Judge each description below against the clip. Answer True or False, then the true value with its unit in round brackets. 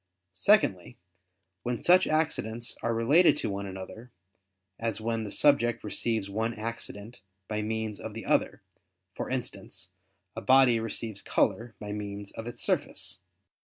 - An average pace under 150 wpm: True (140 wpm)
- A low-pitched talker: True (115 Hz)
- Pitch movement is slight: True (2.3 semitones)